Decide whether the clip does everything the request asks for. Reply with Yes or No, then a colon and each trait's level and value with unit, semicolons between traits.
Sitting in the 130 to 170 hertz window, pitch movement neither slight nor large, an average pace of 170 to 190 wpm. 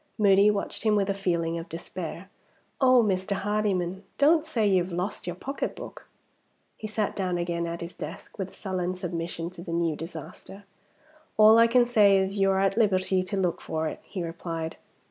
No: high, 190 Hz; average, 3.3 semitones; average, 185 wpm